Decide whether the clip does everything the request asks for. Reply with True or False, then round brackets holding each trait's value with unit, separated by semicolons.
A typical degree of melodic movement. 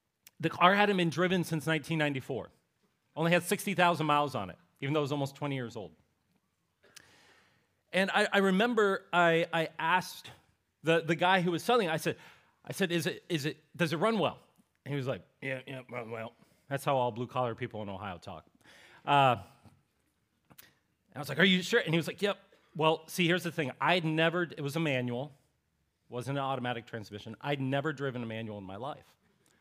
False (5.7 semitones)